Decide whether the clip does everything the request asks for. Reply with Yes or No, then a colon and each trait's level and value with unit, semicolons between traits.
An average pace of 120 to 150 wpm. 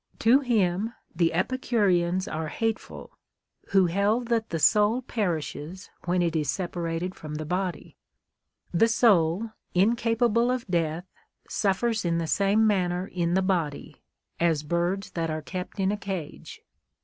Yes: average, 140 wpm